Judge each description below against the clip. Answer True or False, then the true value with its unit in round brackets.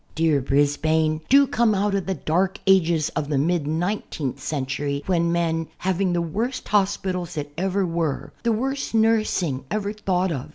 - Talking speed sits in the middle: True (170 wpm)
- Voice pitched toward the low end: False (175 Hz)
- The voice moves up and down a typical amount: True (4.3 semitones)